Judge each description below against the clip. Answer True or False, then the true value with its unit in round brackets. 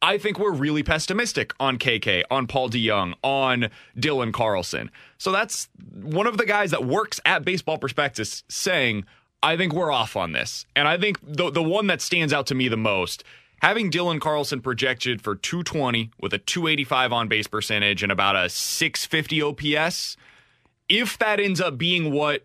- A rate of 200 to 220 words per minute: False (180 wpm)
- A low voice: False (145 Hz)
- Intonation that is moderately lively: False (5.9 semitones)